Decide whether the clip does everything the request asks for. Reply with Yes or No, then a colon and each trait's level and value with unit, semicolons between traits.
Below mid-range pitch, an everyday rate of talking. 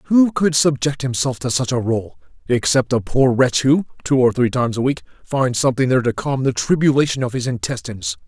No: low, 130 Hz; fast, 210 wpm